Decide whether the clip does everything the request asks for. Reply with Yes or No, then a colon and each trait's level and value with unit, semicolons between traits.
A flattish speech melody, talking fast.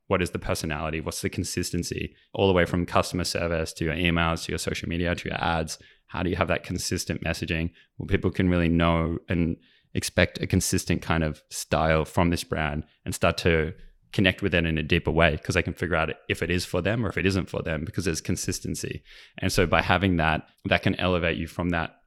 Yes: narrow, 2.3 semitones; fast, 235 wpm